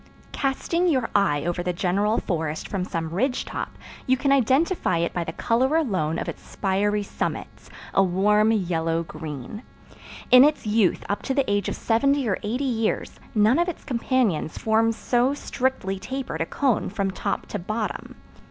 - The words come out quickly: No, average, 170 wpm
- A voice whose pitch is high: Yes, high, 215 Hz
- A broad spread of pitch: Yes, wide, 6.1 semitones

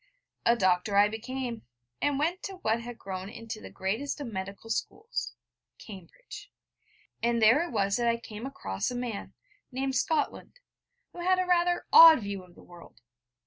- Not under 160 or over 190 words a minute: Yes, average, 170 wpm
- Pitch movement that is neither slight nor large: No, wide, 6.2 semitones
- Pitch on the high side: Yes, high, 235 Hz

